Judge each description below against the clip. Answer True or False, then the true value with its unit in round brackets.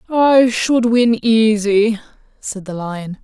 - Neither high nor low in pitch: False (220 Hz)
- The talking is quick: False (130 wpm)